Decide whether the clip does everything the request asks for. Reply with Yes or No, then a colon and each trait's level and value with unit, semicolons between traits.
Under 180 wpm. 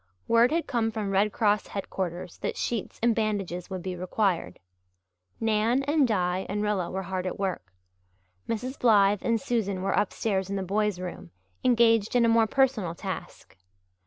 Yes: average, 165 wpm